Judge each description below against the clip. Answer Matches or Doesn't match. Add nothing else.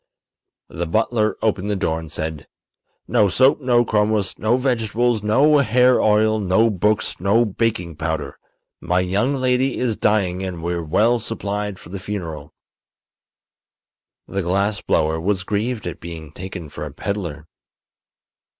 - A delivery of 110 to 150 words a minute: Matches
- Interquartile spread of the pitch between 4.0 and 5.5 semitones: Matches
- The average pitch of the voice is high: Doesn't match